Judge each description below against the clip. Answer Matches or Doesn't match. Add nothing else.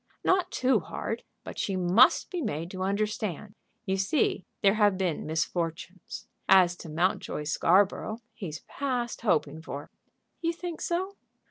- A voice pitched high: Matches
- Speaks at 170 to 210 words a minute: Doesn't match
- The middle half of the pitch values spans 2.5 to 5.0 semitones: Doesn't match